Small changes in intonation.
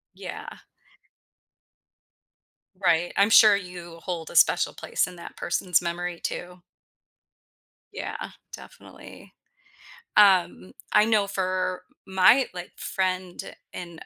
Yes: narrow, 1.7 semitones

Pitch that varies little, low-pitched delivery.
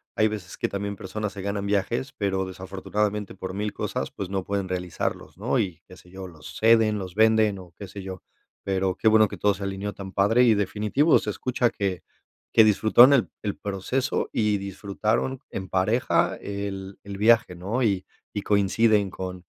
Yes: narrow, 2.2 semitones; low, 100 Hz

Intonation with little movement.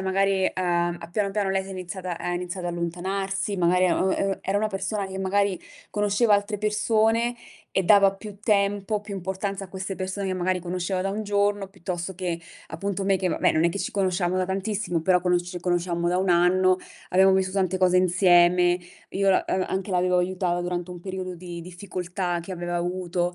Yes: narrow, 1.9 semitones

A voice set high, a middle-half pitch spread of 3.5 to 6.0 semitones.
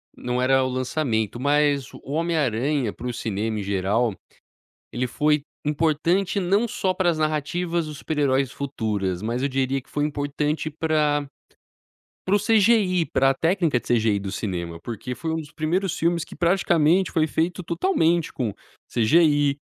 No: medium, 145 Hz; average, 5.1 semitones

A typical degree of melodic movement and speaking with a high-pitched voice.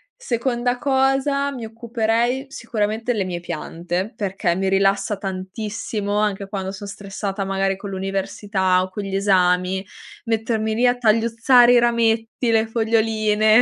Yes: average, 3.2 semitones; high, 215 Hz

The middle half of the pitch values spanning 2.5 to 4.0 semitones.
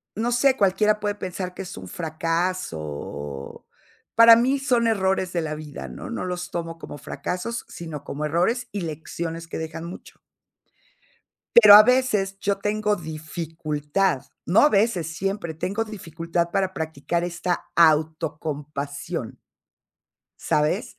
No: average, 4.6 semitones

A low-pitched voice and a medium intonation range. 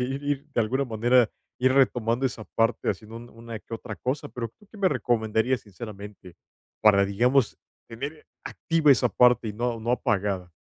Yes: low, 120 Hz; average, 3.1 semitones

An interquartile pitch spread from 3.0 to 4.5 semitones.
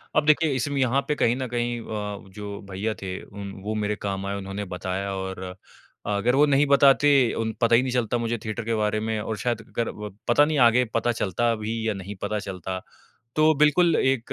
Yes: average, 3.7 semitones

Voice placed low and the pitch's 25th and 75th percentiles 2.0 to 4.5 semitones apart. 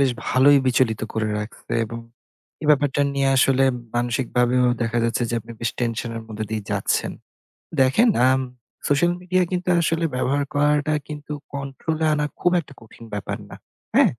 Yes: low, 130 Hz; average, 4.1 semitones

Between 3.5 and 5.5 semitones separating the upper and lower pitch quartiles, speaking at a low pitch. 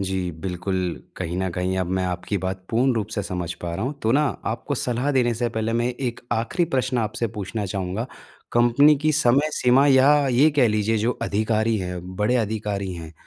Yes: average, 4.8 semitones; low, 110 Hz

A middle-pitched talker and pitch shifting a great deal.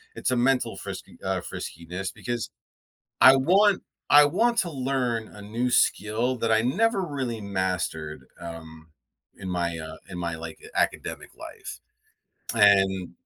No: low, 110 Hz; wide, 6.9 semitones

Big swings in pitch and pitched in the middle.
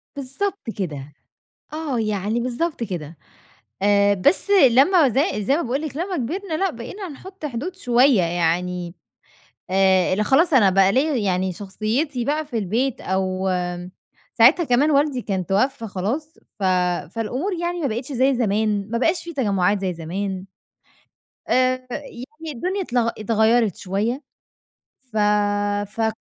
No: wide, 6.8 semitones; high, 235 Hz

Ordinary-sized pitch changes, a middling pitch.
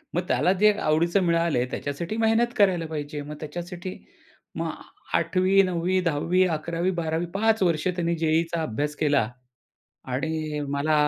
Yes: average, 3.2 semitones; medium, 170 Hz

